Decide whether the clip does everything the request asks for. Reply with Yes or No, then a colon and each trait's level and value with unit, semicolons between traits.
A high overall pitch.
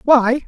Yes: very high, 255 Hz